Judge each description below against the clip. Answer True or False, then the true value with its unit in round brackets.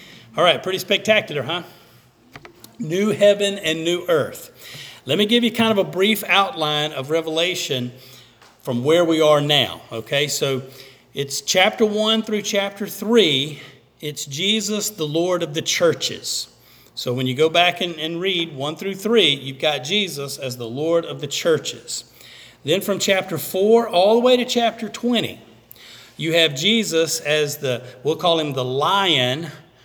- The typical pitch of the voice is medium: True (165 Hz)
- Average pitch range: False (6.3 semitones)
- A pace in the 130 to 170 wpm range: True (165 wpm)